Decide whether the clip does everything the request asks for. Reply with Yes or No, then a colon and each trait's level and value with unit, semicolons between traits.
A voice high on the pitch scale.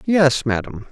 No: low, 135 Hz